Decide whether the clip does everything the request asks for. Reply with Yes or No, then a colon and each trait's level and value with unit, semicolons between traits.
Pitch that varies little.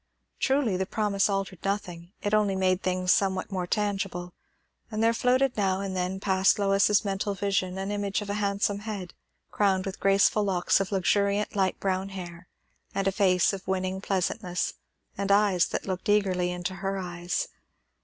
Yes: narrow, 1.6 semitones